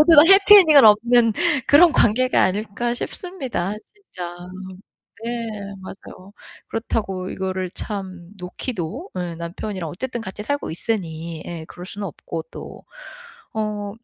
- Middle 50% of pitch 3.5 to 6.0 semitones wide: Yes, wide, 5.4 semitones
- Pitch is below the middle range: No, high, 205 Hz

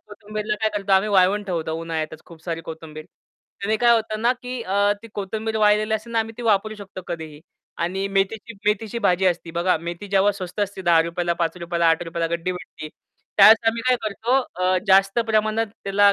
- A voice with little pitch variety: No, average, 4.0 semitones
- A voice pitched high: Yes, high, 195 Hz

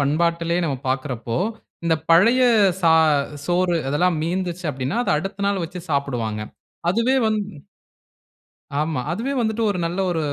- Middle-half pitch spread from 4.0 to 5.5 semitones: Yes, average, 5.0 semitones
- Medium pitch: Yes, medium, 170 Hz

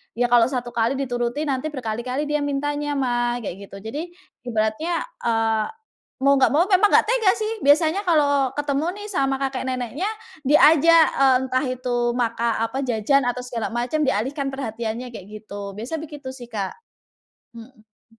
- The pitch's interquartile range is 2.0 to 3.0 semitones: No, average, 3.7 semitones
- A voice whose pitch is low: No, very high, 255 Hz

